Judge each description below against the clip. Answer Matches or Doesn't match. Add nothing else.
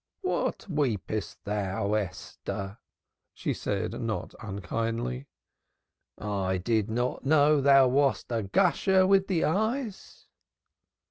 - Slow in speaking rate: Matches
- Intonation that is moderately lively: Doesn't match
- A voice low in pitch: Matches